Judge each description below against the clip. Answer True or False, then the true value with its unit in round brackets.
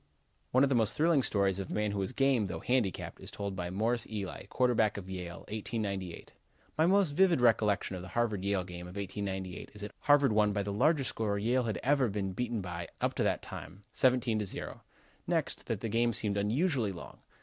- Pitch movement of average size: True (4.1 semitones)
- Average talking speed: False (215 wpm)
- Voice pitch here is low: True (105 Hz)